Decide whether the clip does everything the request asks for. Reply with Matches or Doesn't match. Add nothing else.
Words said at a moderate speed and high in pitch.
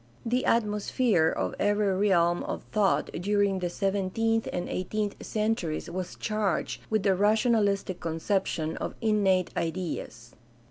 Doesn't match